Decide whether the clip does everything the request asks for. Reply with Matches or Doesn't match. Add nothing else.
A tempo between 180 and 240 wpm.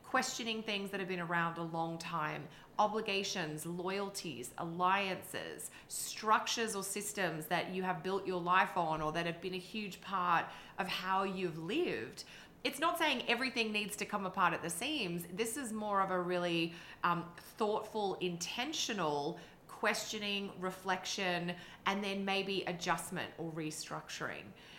Doesn't match